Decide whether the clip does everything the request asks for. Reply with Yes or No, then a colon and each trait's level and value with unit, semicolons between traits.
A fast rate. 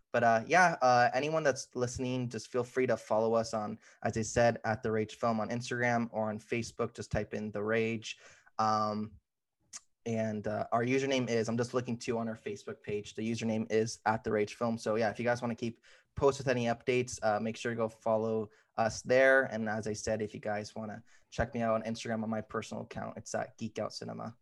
Yes: fast, 235 wpm